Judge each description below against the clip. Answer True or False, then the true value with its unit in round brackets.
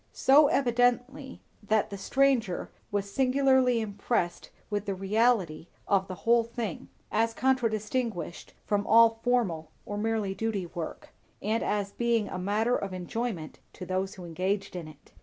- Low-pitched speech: False (215 Hz)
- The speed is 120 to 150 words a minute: True (140 wpm)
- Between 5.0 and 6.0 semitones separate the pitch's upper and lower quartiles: False (3.9 semitones)